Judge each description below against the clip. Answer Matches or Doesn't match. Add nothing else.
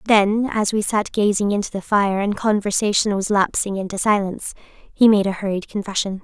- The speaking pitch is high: Matches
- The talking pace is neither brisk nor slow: Matches